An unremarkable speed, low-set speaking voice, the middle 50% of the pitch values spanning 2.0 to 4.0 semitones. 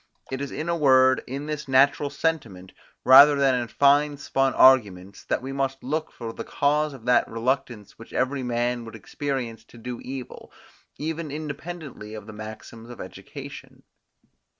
Yes: average, 165 wpm; low, 130 Hz; average, 3.3 semitones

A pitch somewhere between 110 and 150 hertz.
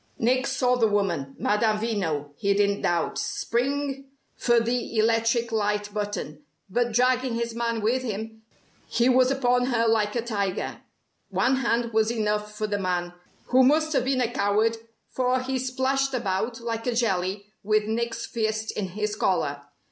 No: high, 225 Hz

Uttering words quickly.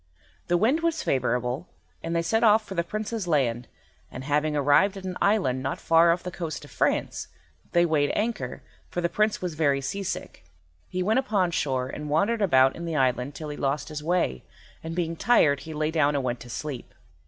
Yes: fast, 210 wpm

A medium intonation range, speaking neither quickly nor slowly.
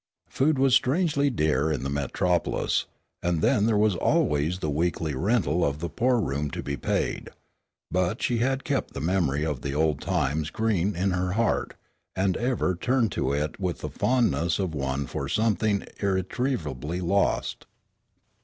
No: wide, 6.8 semitones; average, 165 wpm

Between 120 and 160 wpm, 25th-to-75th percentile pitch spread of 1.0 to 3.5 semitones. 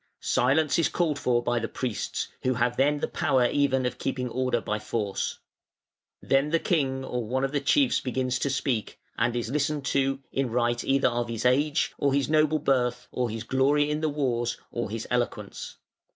No: average, 195 wpm; average, 2.9 semitones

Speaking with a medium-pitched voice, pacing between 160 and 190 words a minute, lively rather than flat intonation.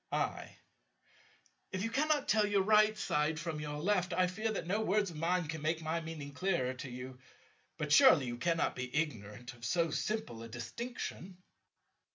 Yes: medium, 165 Hz; average, 180 wpm; wide, 6.1 semitones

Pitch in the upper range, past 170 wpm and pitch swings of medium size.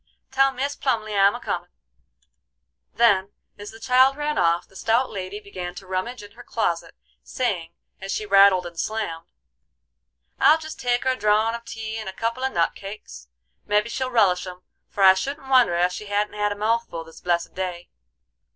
Yes: high, 210 Hz; average, 190 wpm; average, 4.3 semitones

